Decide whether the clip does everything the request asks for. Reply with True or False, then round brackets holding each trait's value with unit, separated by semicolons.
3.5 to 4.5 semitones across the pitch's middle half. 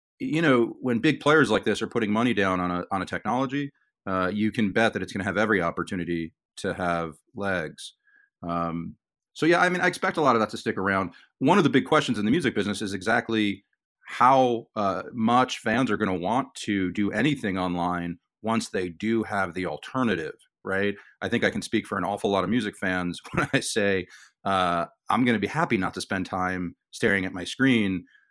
True (4.2 semitones)